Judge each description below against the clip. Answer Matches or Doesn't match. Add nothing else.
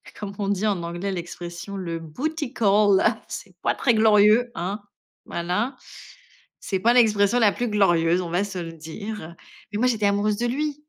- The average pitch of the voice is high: Matches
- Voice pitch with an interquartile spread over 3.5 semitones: Matches